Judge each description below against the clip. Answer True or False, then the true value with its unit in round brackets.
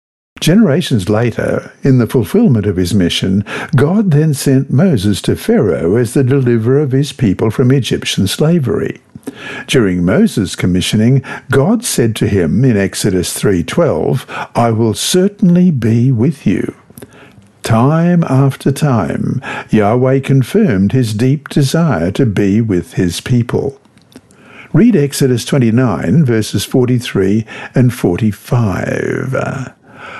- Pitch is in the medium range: False (125 Hz)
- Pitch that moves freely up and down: False (4.8 semitones)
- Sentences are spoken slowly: True (115 wpm)